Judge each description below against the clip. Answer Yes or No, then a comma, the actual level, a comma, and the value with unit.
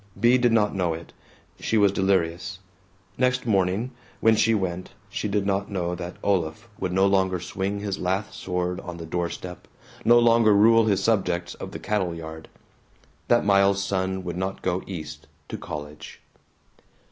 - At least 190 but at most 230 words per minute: No, average, 170 wpm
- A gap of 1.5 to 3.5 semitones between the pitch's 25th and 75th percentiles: Yes, average, 2.8 semitones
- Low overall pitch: Yes, very low, 95 Hz